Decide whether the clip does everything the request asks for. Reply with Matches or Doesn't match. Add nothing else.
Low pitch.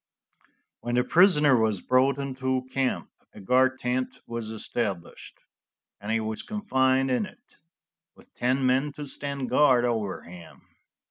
Matches